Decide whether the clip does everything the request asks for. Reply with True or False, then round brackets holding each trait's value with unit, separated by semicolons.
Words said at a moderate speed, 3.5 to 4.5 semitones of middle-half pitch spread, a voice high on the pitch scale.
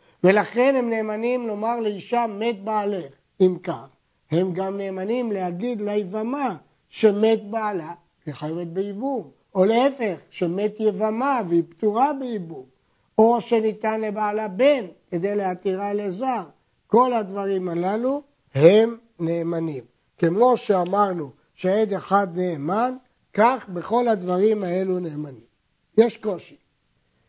True (110 wpm; 4.2 semitones; 205 Hz)